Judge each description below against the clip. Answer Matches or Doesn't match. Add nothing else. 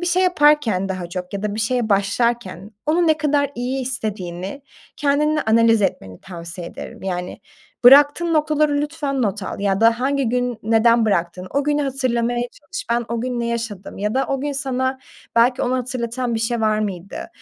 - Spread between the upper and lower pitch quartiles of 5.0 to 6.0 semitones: Matches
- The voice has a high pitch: Matches